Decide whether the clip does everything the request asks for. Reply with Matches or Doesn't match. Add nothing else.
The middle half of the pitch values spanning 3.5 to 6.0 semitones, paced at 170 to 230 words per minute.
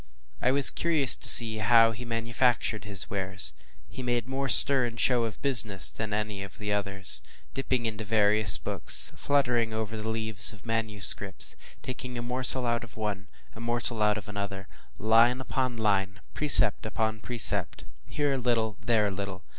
Doesn't match